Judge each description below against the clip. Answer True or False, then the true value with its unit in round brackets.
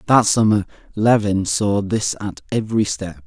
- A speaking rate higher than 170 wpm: False (145 wpm)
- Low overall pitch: True (105 Hz)